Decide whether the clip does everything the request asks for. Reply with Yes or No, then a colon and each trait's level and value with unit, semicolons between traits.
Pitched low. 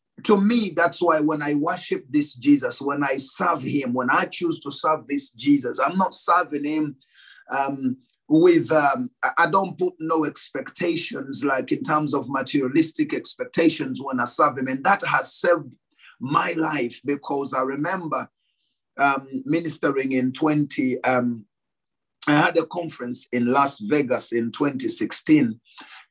No: medium, 155 Hz